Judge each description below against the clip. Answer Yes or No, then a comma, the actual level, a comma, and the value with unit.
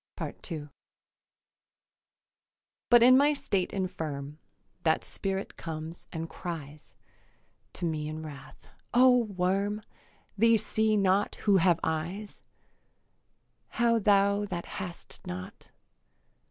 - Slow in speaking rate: Yes, slow, 100 wpm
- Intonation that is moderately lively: Yes, average, 4.7 semitones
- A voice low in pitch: No, medium, 185 Hz